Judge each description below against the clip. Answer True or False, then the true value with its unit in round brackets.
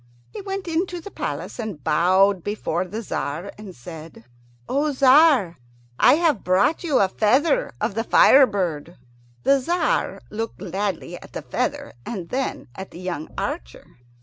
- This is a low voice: False (210 Hz)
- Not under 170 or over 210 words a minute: False (155 wpm)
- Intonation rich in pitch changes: True (7.8 semitones)